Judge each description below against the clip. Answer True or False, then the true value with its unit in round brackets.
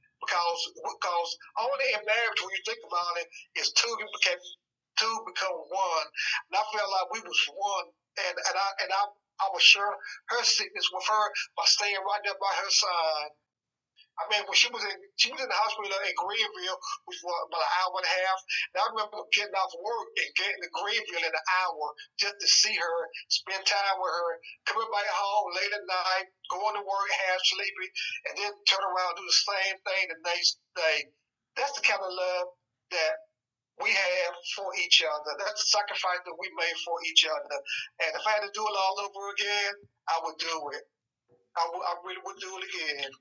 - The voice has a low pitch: False (195 Hz)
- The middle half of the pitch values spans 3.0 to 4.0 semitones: True (3.4 semitones)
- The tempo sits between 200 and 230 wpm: True (205 wpm)